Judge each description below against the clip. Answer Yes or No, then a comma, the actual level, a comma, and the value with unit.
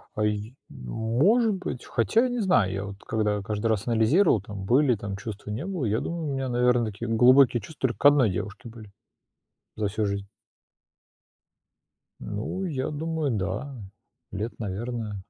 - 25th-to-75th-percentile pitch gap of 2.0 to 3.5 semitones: No, average, 5.3 semitones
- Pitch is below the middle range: Yes, low, 115 Hz